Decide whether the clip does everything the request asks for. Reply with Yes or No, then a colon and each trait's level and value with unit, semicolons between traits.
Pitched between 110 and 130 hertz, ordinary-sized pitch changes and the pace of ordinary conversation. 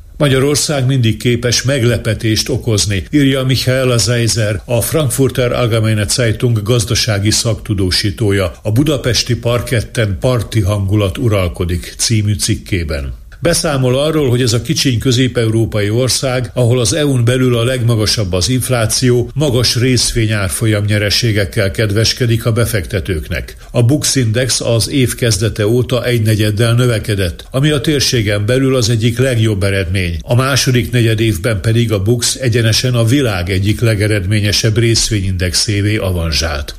Yes: low, 115 Hz; average, 3.2 semitones; average, 120 wpm